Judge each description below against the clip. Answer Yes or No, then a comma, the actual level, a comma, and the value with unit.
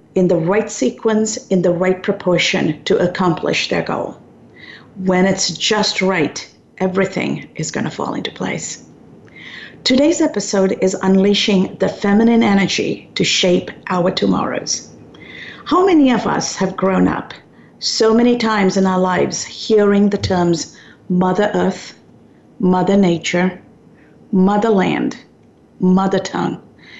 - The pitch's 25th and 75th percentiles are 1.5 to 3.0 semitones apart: Yes, narrow, 2.5 semitones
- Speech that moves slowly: Yes, slow, 125 wpm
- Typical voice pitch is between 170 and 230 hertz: Yes, high, 190 Hz